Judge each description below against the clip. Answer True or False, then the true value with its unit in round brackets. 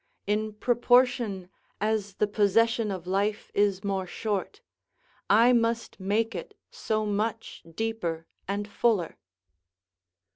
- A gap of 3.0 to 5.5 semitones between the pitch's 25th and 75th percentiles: False (2.4 semitones)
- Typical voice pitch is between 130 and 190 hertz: False (210 Hz)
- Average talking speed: False (110 wpm)